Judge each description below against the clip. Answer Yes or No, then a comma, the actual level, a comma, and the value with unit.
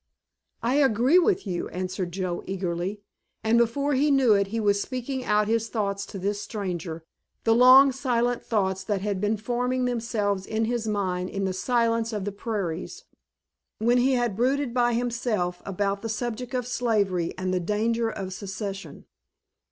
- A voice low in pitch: No, high, 220 Hz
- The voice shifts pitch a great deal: No, average, 3.9 semitones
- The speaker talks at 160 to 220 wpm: Yes, average, 165 wpm